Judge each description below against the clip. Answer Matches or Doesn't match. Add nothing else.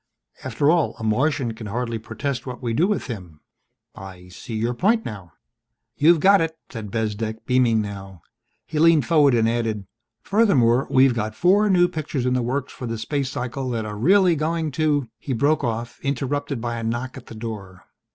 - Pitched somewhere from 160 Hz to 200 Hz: Doesn't match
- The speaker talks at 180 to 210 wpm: Matches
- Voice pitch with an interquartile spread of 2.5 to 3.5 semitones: Doesn't match